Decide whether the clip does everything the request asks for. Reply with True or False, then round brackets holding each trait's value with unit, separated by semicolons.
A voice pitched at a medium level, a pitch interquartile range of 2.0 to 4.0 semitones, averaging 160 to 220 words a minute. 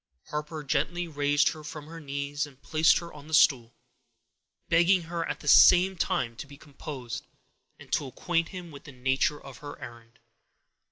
True (150 Hz; 3.2 semitones; 175 wpm)